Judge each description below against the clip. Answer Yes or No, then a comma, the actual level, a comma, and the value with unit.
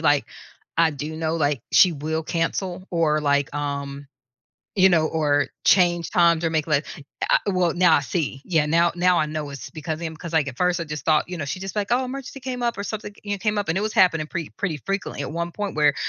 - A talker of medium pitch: Yes, medium, 165 Hz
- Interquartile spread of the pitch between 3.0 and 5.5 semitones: Yes, average, 3.4 semitones